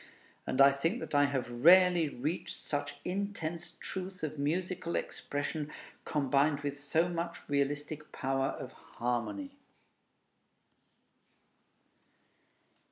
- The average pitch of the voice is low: No, medium, 150 Hz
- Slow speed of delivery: Yes, slow, 100 wpm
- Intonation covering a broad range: No, average, 3.6 semitones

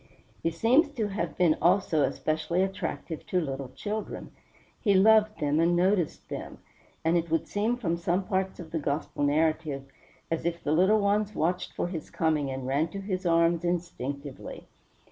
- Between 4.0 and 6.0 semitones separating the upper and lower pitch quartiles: No, average, 3.6 semitones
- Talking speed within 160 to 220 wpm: Yes, average, 170 wpm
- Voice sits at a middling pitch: Yes, medium, 170 Hz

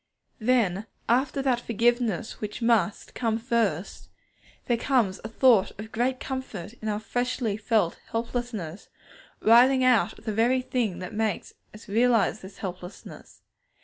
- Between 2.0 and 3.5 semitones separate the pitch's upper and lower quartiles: Yes, average, 3.0 semitones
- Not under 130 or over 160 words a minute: Yes, average, 140 wpm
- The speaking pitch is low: No, high, 225 Hz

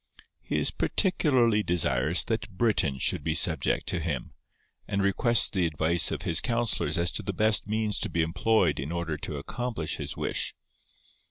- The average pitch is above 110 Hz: No, very low, 90 Hz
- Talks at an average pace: Yes, average, 170 wpm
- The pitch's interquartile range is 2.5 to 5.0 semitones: No, wide, 5.6 semitones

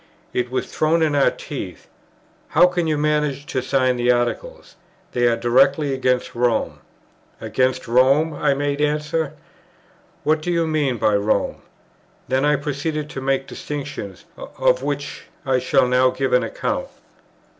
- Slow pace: No, average, 155 wpm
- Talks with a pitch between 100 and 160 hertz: Yes, low, 135 Hz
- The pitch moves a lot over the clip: No, average, 3.0 semitones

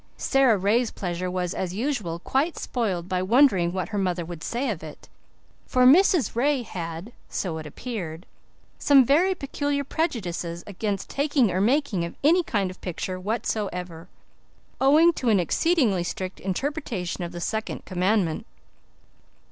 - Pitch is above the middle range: Yes, high, 205 Hz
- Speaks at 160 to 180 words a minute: No, average, 150 wpm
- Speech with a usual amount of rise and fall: No, wide, 7.1 semitones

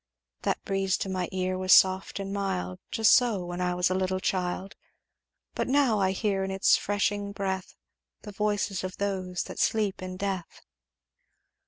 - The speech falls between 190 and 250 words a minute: No, average, 170 wpm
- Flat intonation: Yes, narrow, 1.5 semitones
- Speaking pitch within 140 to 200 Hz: Yes, high, 190 Hz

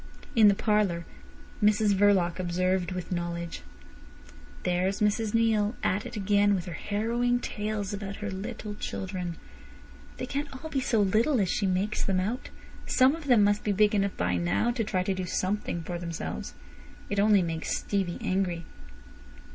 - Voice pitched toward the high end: Yes, high, 200 Hz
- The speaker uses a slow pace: No, average, 165 wpm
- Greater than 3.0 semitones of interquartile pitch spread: No, average, 2.7 semitones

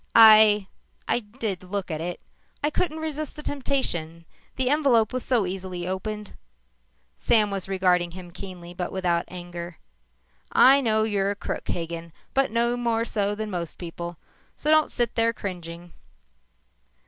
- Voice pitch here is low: No, high, 200 Hz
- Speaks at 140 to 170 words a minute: Yes, average, 150 wpm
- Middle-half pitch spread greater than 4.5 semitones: Yes, average, 5.1 semitones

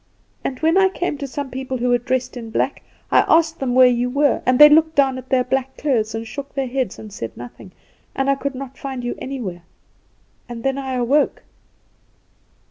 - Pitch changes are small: Yes, narrow, 2.3 semitones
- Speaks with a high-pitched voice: Yes, very high, 260 Hz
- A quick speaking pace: Yes, fast, 210 wpm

